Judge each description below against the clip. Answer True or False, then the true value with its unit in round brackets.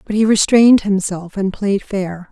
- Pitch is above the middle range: True (200 Hz)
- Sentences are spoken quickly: False (180 wpm)